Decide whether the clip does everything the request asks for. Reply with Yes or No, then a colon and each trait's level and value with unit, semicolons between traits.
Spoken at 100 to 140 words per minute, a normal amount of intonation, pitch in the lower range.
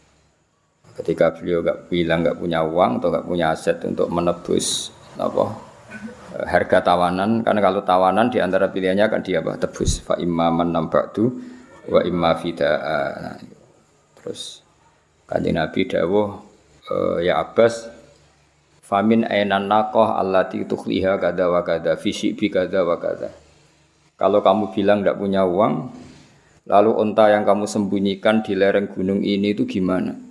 No: average, 135 wpm; narrow, 2.3 semitones; low, 100 Hz